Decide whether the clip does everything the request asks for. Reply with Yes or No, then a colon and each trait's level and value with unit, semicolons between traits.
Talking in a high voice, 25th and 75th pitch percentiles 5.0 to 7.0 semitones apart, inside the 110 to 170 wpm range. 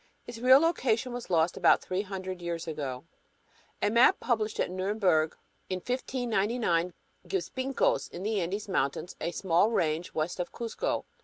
Yes: high, 195 Hz; wide, 5.6 semitones; average, 155 wpm